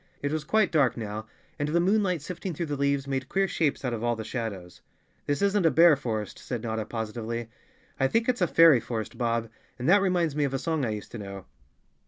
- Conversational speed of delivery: No, fast, 230 wpm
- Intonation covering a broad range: Yes, wide, 6.5 semitones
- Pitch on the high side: No, low, 135 Hz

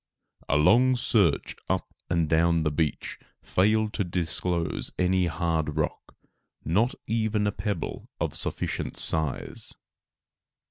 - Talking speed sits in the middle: No, slow, 120 wpm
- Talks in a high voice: No, very low, 90 Hz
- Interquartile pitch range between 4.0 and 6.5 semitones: Yes, average, 4.6 semitones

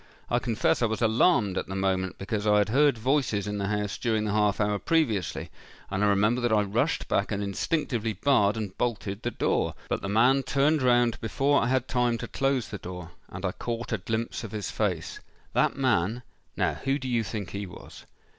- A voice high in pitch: No, low, 110 Hz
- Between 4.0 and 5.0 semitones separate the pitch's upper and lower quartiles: No, average, 3.4 semitones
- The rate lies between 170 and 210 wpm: Yes, fast, 205 wpm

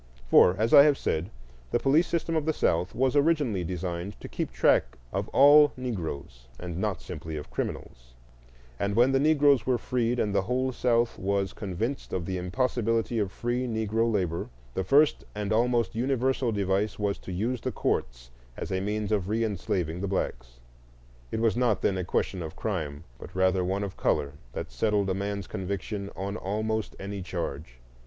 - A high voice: No, low, 100 Hz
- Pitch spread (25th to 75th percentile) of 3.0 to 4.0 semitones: No, average, 4.7 semitones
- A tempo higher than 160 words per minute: Yes, average, 175 wpm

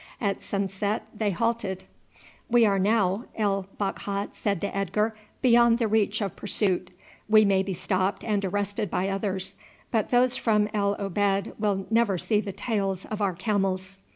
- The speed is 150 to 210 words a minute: Yes, average, 160 wpm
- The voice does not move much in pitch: Yes, narrow, 1.9 semitones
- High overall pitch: Yes, high, 200 Hz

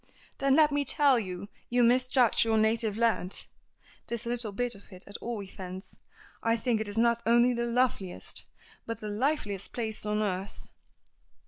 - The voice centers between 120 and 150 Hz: No, high, 230 Hz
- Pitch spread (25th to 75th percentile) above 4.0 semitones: No, average, 3.0 semitones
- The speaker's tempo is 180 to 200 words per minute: No, average, 160 wpm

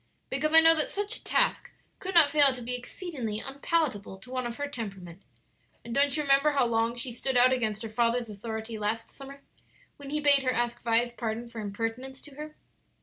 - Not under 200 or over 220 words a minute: Yes, fast, 205 wpm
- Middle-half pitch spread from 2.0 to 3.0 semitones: No, average, 4.0 semitones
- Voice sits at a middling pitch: No, very high, 250 Hz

